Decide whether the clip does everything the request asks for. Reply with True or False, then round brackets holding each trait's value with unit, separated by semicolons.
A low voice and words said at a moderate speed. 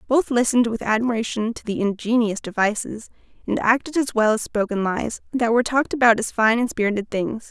False (230 Hz; 190 wpm)